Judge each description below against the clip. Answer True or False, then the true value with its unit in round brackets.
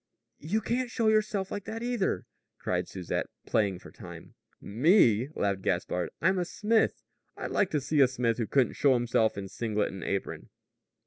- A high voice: False (135 Hz)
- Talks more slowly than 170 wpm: False (175 wpm)